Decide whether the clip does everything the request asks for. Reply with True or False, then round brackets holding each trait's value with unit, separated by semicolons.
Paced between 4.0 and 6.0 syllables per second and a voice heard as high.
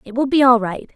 True (5.9 syllables/s; 245 Hz)